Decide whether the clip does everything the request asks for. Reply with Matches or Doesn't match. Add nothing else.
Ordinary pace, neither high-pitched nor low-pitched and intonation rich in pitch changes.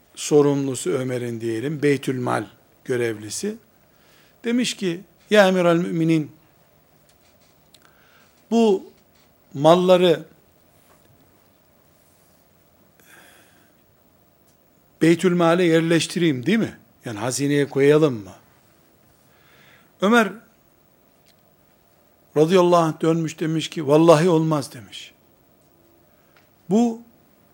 Doesn't match